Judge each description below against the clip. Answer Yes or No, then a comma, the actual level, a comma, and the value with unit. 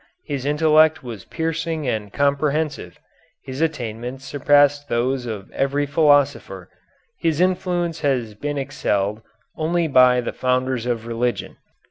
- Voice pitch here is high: No, medium, 140 Hz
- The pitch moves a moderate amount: Yes, average, 4.0 semitones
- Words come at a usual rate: No, slow, 120 wpm